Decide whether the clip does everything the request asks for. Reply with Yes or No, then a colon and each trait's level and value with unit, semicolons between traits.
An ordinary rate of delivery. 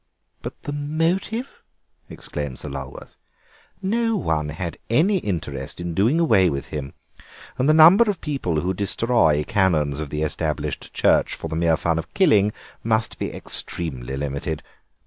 Yes: average, 150 wpm